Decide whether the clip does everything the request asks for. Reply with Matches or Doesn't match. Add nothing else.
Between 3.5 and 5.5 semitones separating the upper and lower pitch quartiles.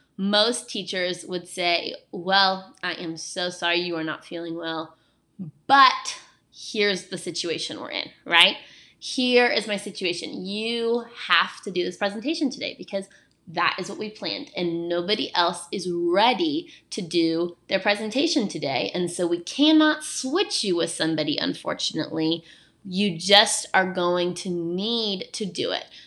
Matches